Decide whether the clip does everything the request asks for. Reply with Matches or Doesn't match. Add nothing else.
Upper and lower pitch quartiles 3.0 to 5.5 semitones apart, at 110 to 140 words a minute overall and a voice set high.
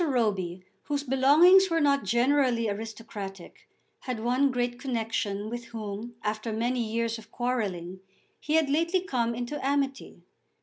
Matches